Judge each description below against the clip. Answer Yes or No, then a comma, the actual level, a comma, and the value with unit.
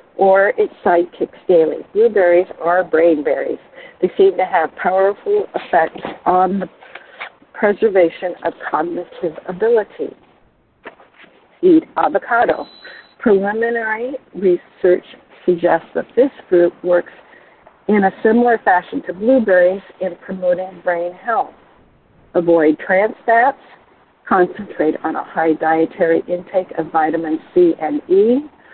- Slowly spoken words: Yes, slow, 110 wpm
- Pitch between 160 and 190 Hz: Yes, medium, 185 Hz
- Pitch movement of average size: Yes, average, 5.0 semitones